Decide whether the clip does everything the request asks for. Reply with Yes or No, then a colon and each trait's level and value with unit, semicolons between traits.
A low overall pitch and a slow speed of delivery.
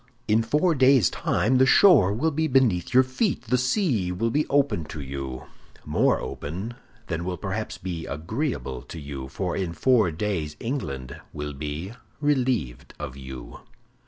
No: very low, 95 Hz; average, 155 wpm